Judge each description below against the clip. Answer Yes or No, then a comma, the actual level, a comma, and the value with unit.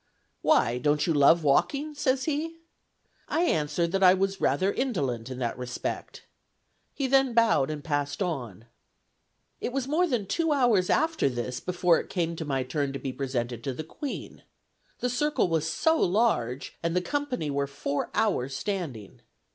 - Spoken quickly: No, average, 170 wpm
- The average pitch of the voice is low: No, medium, 170 Hz